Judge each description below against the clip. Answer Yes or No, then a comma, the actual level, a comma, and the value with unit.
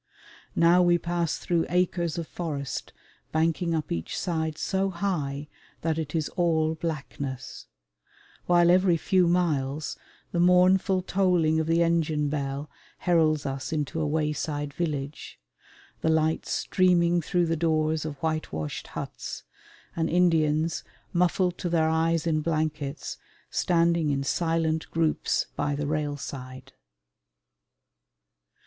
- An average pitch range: No, narrow, 2.3 semitones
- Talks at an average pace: No, slow, 125 wpm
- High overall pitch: No, medium, 160 Hz